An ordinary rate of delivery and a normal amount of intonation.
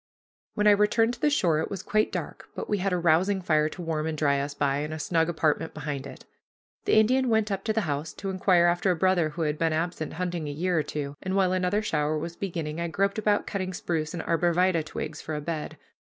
No: fast, 250 wpm; average, 3.9 semitones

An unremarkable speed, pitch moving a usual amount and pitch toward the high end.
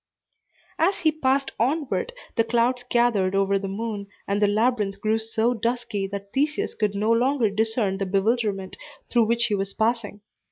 Yes: average, 165 wpm; average, 3.3 semitones; high, 225 Hz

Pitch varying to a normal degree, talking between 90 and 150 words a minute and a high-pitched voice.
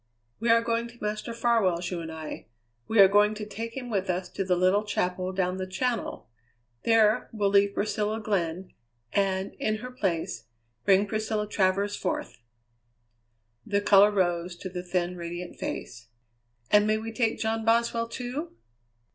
No: average, 3.3 semitones; average, 165 wpm; high, 205 Hz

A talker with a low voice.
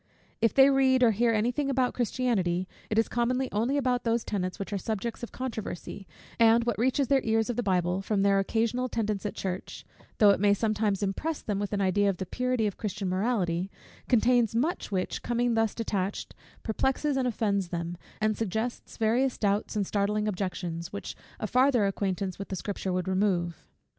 No: high, 215 Hz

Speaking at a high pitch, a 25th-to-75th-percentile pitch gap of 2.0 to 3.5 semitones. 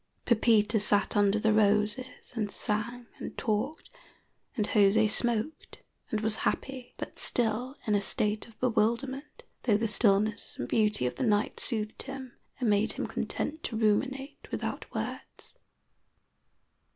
Yes: high, 220 Hz; average, 2.7 semitones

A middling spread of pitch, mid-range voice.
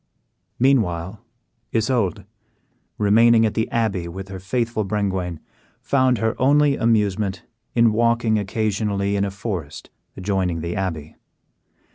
No: average, 3.4 semitones; low, 105 Hz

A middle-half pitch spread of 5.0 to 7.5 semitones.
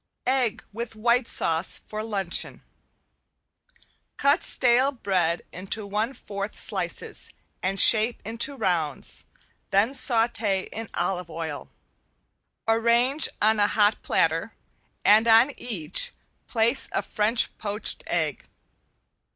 No: average, 3.3 semitones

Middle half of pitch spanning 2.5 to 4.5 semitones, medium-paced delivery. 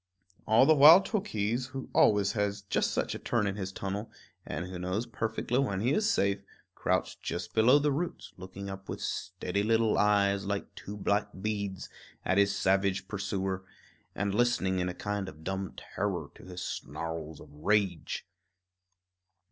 Yes: average, 2.8 semitones; average, 165 wpm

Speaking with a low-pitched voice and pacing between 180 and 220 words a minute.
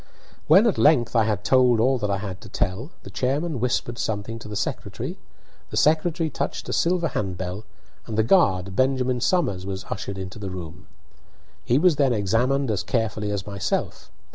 Yes: low, 115 Hz; average, 185 wpm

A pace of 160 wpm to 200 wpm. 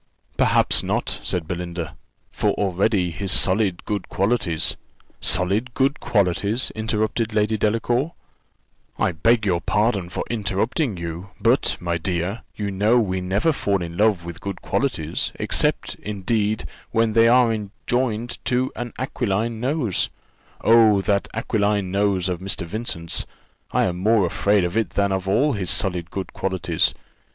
No: average, 145 wpm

